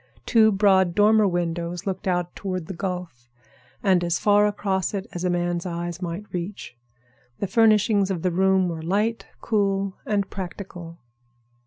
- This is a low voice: No, high, 190 Hz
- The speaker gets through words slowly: No, average, 155 wpm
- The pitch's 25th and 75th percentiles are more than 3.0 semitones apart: No, narrow, 2.6 semitones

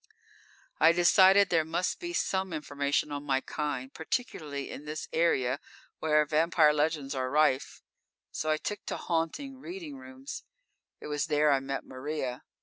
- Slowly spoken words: No, average, 155 wpm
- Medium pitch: Yes, medium, 155 Hz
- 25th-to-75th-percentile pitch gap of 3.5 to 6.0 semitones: Yes, average, 3.8 semitones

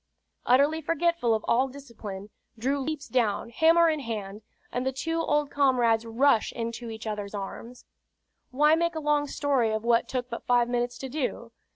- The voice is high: Yes, very high, 250 Hz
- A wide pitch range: No, average, 4.2 semitones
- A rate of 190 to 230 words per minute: No, average, 175 wpm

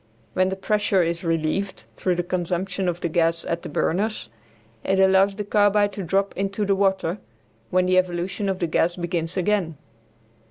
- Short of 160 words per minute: No, average, 175 wpm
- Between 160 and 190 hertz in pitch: Yes, medium, 185 Hz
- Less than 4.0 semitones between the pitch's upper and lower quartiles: Yes, narrow, 2.4 semitones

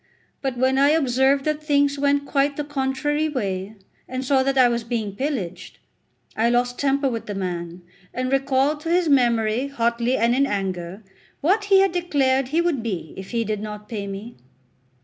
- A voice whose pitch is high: Yes, very high, 260 Hz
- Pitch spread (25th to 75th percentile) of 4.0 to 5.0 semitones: Yes, average, 4.3 semitones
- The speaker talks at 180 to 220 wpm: Yes, average, 185 wpm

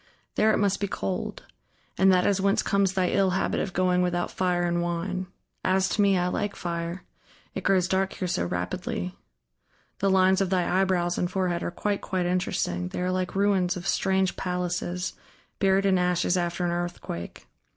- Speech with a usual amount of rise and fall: No, narrow, 1.6 semitones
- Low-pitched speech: No, medium, 185 Hz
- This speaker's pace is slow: No, average, 185 wpm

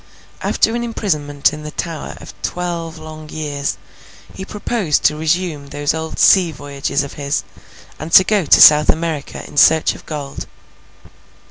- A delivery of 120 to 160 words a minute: Yes, average, 155 wpm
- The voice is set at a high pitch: No, medium, 155 Hz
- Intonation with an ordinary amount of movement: Yes, average, 3.0 semitones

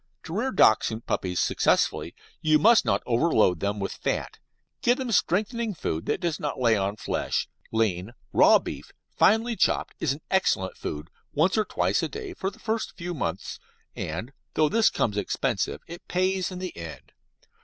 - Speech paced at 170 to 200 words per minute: Yes, average, 175 wpm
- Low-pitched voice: No, medium, 155 Hz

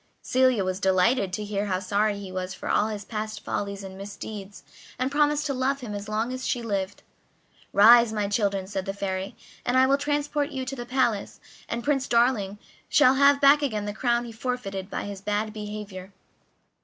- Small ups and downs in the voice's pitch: No, average, 4.3 semitones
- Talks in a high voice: Yes, high, 215 Hz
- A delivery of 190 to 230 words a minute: Yes, average, 195 wpm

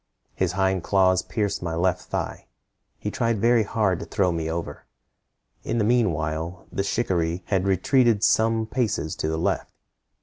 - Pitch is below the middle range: Yes, very low, 95 Hz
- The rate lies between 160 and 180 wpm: Yes, average, 165 wpm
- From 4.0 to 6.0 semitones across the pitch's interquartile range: Yes, average, 4.6 semitones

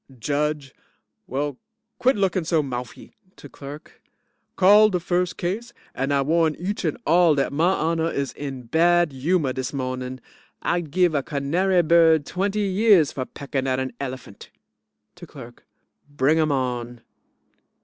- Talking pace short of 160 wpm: Yes, average, 150 wpm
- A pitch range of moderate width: Yes, average, 4.6 semitones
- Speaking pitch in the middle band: Yes, medium, 155 Hz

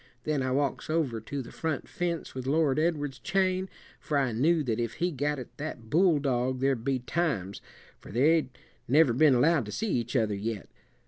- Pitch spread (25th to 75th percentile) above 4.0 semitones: Yes, average, 4.7 semitones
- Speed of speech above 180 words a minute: Yes, average, 190 wpm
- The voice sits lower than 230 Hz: Yes, medium, 140 Hz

